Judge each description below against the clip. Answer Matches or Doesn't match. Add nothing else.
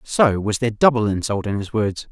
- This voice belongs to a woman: Doesn't match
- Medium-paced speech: Doesn't match